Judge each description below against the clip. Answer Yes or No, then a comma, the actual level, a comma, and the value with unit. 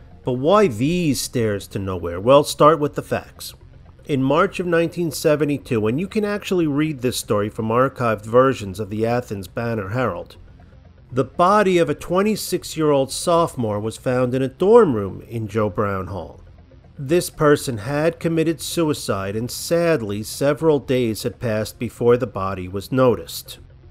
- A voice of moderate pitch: No, low, 125 Hz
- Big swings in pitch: Yes, wide, 6.0 semitones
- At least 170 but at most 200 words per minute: No, average, 160 wpm